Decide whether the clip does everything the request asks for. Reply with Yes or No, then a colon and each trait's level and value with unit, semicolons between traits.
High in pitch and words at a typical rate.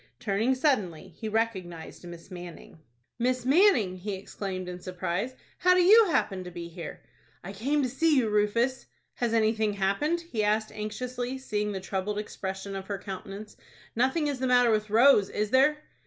Yes: high, 215 Hz; average, 170 wpm